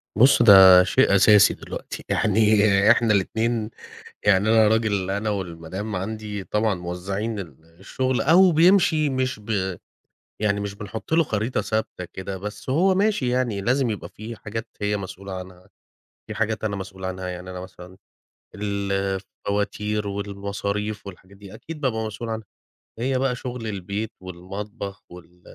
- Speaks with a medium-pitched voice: No, low, 105 Hz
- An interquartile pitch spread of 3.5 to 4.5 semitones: No, average, 2.7 semitones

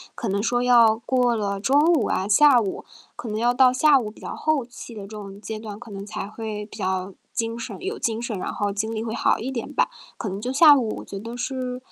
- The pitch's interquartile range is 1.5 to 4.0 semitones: Yes, average, 3.3 semitones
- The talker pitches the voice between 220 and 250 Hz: Yes, high, 225 Hz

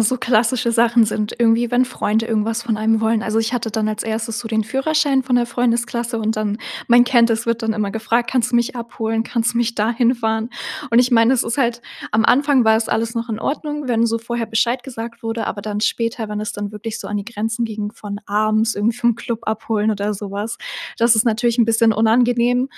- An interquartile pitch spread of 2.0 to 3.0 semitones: No, narrow, 1.5 semitones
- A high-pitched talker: Yes, high, 230 Hz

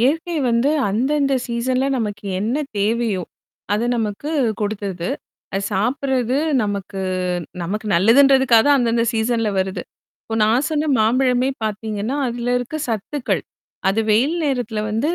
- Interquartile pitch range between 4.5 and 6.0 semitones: No, average, 3.8 semitones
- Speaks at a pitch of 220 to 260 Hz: Yes, high, 230 Hz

